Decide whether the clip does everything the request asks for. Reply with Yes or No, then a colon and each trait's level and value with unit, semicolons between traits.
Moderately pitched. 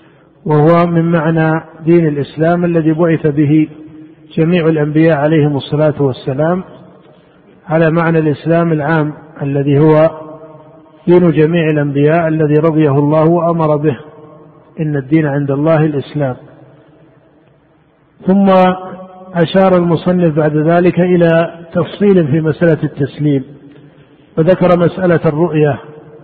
Yes: medium, 155 Hz